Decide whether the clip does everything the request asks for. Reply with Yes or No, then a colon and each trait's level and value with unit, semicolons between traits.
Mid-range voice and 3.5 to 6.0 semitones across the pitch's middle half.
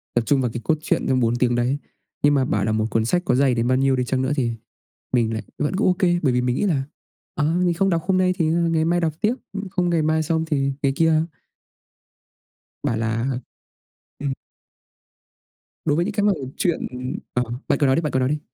Yes: medium, 145 Hz; average, 5.1 semitones